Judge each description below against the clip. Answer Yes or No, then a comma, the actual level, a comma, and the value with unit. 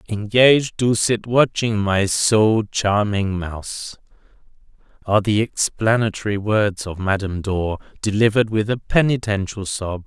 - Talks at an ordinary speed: No, slow, 120 wpm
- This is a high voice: No, low, 105 Hz